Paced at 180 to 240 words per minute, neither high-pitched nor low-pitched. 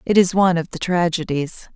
Yes: fast, 205 wpm; medium, 175 Hz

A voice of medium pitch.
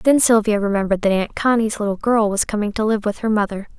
No: high, 210 Hz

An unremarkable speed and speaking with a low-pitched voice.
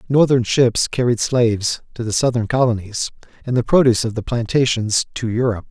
Yes: average, 170 wpm; low, 120 Hz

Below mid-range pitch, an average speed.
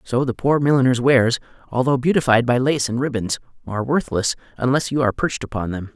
Yes: low, 125 Hz; average, 190 wpm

